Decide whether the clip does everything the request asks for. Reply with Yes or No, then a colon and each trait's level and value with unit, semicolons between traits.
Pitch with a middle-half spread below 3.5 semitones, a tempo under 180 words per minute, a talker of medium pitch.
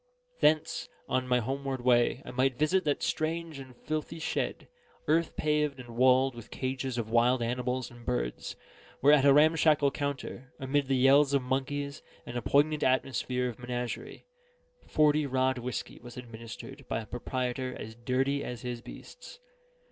No: average, 2.7 semitones; average, 165 wpm; low, 130 Hz